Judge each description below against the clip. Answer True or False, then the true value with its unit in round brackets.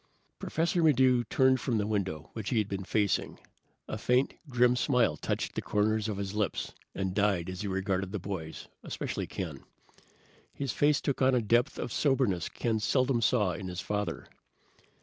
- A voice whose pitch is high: False (105 Hz)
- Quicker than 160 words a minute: True (175 wpm)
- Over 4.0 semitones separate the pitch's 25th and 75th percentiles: True (4.5 semitones)